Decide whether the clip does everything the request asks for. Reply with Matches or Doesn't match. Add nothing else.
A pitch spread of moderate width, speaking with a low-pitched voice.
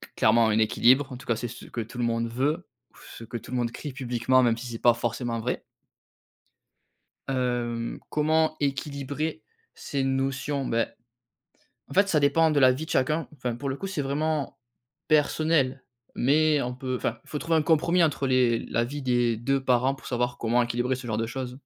Matches